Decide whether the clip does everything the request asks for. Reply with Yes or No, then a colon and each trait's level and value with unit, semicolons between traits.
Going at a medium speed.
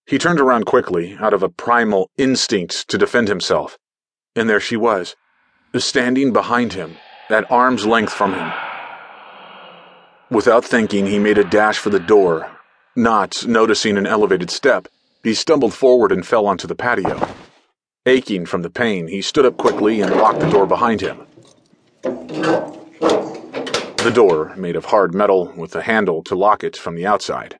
Yes: average, 165 wpm